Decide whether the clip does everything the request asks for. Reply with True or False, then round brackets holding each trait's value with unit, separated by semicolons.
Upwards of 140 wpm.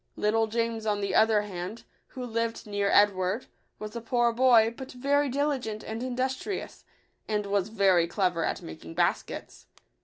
True (155 wpm)